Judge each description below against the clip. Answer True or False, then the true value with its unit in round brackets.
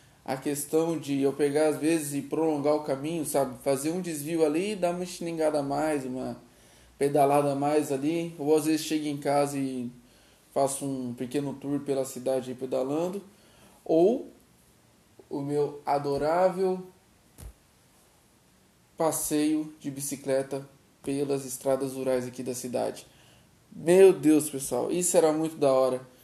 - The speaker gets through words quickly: False (140 wpm)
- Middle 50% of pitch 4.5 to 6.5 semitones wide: False (2.7 semitones)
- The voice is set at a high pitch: False (145 Hz)